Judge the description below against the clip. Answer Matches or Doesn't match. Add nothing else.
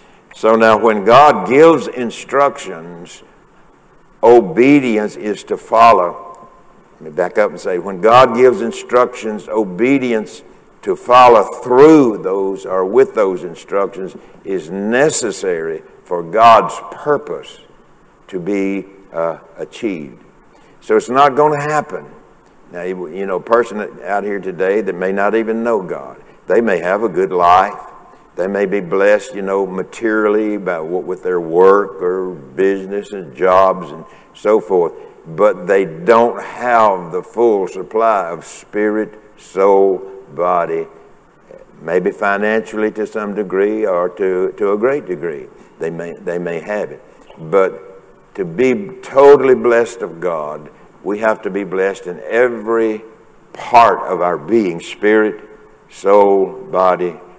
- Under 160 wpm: Matches